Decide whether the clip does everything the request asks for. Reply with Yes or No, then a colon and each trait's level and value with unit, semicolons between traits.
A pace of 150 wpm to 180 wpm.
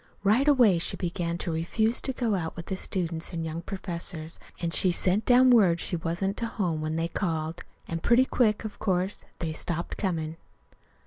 No: average, 190 wpm